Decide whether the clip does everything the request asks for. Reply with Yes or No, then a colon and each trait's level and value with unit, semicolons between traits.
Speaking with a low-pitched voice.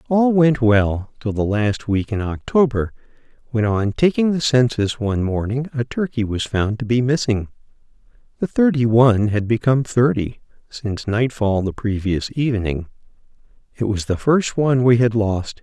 Yes: low, 120 Hz